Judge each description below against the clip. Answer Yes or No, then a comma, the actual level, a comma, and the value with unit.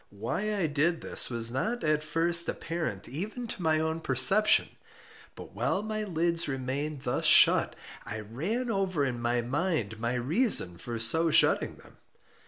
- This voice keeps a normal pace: Yes, average, 160 wpm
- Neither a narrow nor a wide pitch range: No, wide, 6.9 semitones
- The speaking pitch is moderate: Yes, medium, 155 Hz